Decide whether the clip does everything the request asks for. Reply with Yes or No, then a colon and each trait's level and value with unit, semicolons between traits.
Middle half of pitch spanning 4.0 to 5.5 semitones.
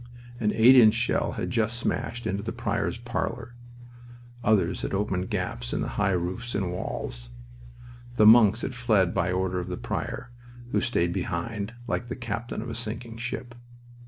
Yes: average, 4.3 semitones